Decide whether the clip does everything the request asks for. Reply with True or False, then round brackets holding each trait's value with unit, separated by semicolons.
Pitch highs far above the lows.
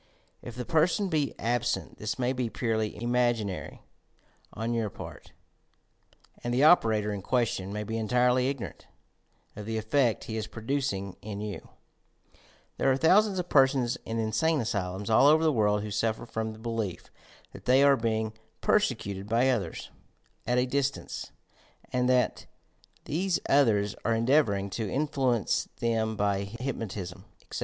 False (3.7 semitones)